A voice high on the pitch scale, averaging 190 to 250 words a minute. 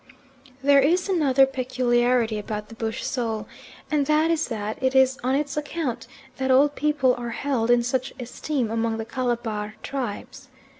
No: very high, 255 Hz; average, 160 wpm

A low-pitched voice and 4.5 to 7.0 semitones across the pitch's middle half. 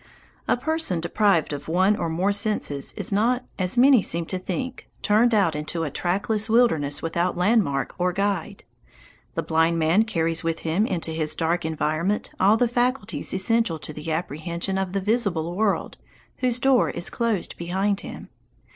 No: medium, 185 Hz; average, 4.9 semitones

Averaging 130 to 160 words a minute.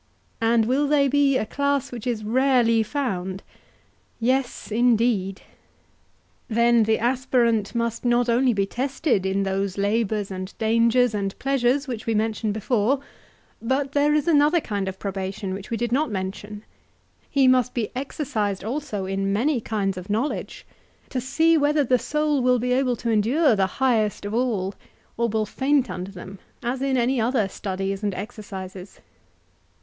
Yes: average, 155 wpm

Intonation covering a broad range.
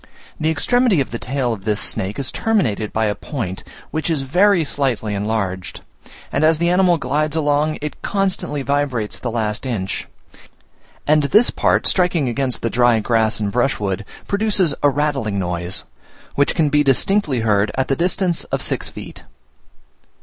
Yes: wide, 6.3 semitones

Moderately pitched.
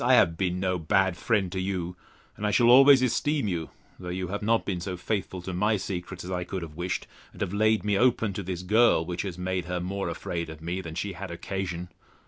No: very low, 95 Hz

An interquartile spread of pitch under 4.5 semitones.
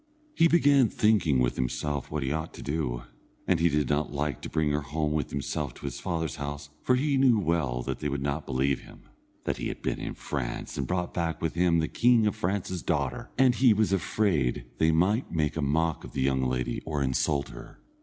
No: average, 4.9 semitones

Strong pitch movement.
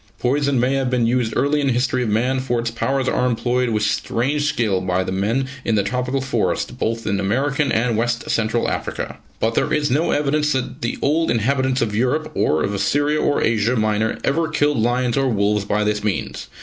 No: average, 3.7 semitones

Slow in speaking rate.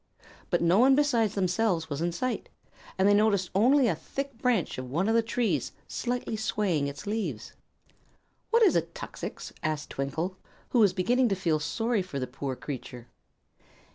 No: average, 170 wpm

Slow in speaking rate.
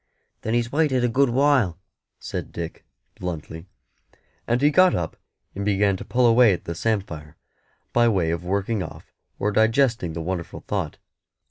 No: average, 160 wpm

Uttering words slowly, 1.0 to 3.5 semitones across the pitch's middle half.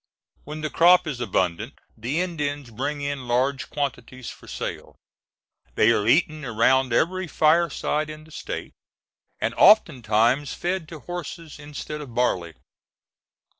No: slow, 130 wpm; average, 4.3 semitones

